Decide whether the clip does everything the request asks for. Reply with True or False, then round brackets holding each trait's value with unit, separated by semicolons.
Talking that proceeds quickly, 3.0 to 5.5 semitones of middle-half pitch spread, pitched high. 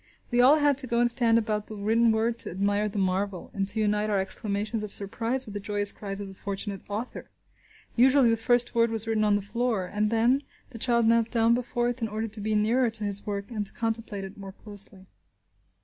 False (230 wpm; 2.5 semitones; 215 Hz)